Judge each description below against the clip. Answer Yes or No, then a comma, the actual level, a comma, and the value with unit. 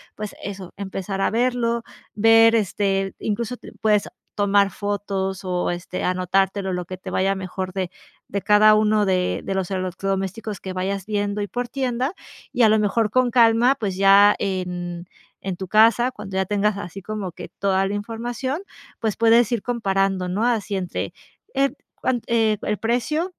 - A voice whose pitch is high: Yes, high, 205 Hz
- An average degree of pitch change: Yes, average, 3.0 semitones